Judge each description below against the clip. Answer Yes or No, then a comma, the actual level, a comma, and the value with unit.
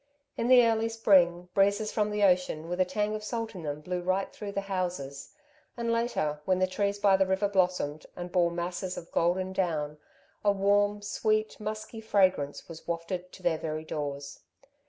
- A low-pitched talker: No, medium, 185 Hz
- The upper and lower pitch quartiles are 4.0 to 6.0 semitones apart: No, average, 3.3 semitones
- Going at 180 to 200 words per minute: Yes, average, 185 wpm